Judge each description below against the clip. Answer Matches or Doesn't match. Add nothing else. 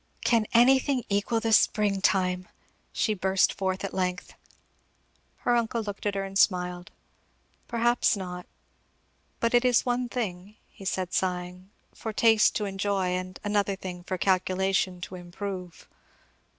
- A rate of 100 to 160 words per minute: Matches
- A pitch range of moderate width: Matches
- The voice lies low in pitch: Doesn't match